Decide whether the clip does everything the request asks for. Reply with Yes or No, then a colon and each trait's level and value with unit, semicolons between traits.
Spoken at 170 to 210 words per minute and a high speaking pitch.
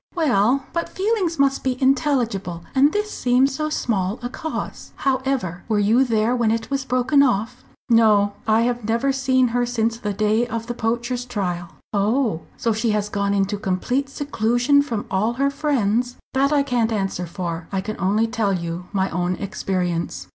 Yes: average, 175 wpm; high, 230 Hz